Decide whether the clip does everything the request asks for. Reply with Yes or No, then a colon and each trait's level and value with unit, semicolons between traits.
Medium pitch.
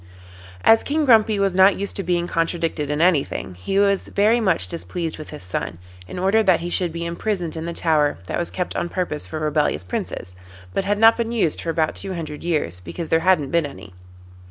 Yes: medium, 170 Hz